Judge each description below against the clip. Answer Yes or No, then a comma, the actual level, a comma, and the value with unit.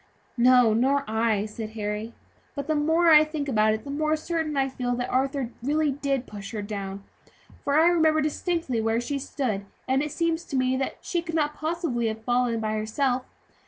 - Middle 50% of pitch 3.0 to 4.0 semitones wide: No, wide, 5.5 semitones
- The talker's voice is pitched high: Yes, very high, 265 Hz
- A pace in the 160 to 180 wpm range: No, average, 195 wpm